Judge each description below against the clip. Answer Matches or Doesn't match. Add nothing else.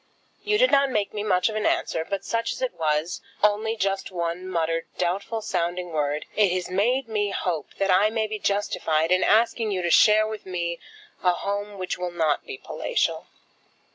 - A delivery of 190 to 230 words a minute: Matches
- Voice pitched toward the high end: Matches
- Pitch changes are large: Doesn't match